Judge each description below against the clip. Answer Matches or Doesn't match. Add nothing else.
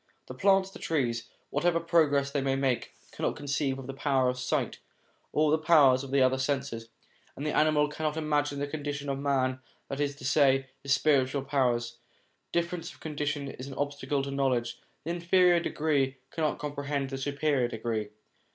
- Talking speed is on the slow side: Doesn't match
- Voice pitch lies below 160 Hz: Matches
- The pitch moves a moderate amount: Doesn't match